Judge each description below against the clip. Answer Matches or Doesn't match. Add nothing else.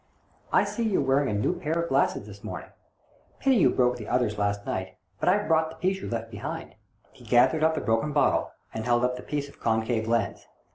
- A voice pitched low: Matches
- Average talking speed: Doesn't match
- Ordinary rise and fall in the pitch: Doesn't match